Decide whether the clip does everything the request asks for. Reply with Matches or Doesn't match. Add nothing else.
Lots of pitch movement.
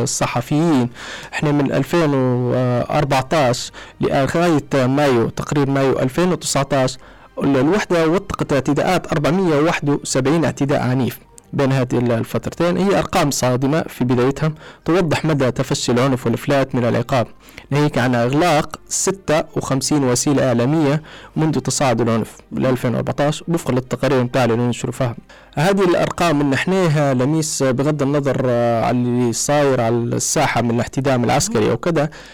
Doesn't match